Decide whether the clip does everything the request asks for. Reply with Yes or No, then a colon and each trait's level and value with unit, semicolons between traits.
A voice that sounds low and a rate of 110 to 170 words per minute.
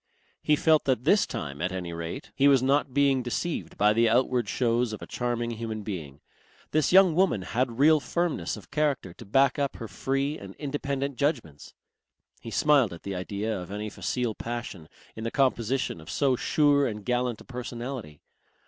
No: low, 125 Hz; average, 185 wpm